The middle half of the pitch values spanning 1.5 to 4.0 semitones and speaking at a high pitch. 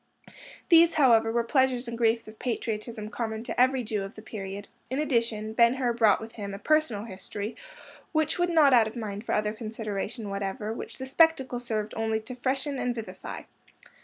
Yes: average, 3.2 semitones; high, 230 Hz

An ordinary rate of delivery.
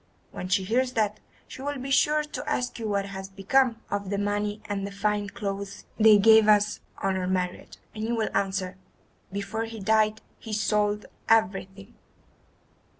Yes: average, 170 wpm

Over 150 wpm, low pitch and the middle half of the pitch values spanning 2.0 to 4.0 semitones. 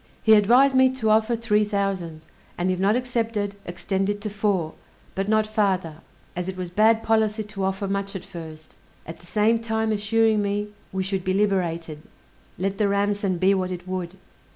No: average, 185 wpm; high, 200 Hz; narrow, 2.6 semitones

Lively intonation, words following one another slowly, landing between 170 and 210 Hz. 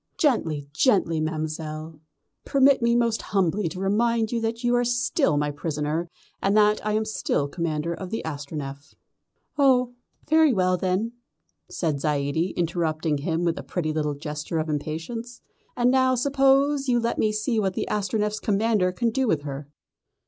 No: wide, 7.0 semitones; average, 165 wpm; high, 190 Hz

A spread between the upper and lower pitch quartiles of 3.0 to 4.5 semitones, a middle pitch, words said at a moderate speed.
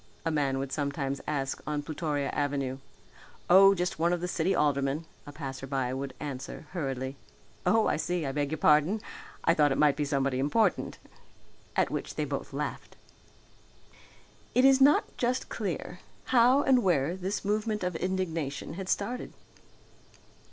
No: average, 5.3 semitones; medium, 155 Hz; average, 150 wpm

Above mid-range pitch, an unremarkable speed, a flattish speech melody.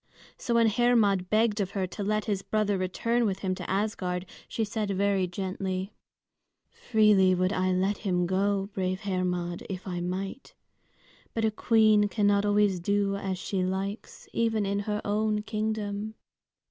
Yes: high, 200 Hz; average, 160 wpm; narrow, 2.3 semitones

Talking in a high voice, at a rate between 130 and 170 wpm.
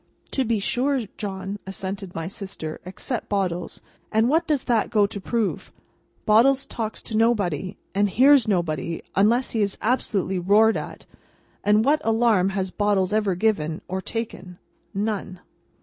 Yes: high, 205 Hz; average, 150 wpm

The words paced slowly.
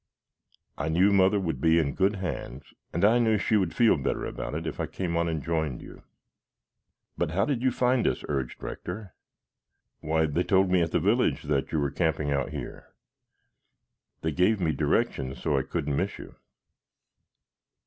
No: average, 180 wpm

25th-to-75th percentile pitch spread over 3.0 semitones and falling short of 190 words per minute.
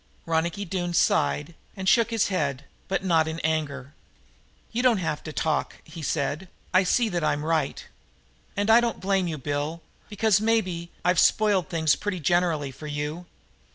Yes: average, 4.1 semitones; average, 165 wpm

